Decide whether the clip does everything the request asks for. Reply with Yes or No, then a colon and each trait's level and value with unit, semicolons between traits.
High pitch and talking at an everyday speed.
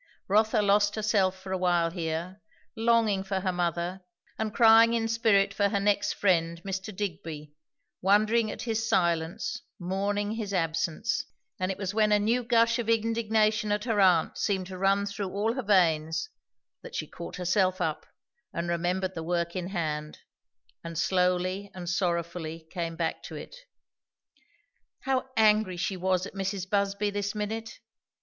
Yes: high, 195 Hz; average, 160 wpm